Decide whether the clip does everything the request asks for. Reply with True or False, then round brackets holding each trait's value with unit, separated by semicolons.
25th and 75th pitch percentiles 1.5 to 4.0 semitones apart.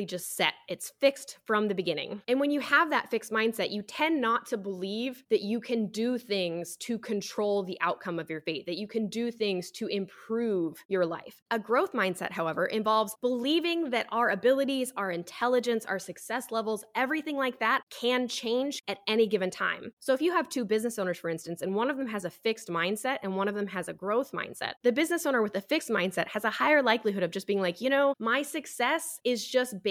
False (4.4 semitones)